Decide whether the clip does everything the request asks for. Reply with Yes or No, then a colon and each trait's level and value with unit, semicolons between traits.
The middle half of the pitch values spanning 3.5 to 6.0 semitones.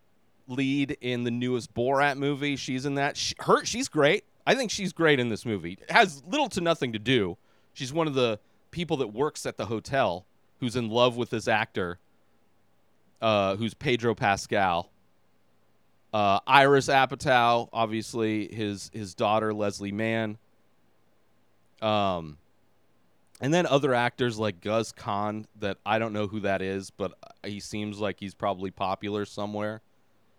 Yes: average, 4.2 semitones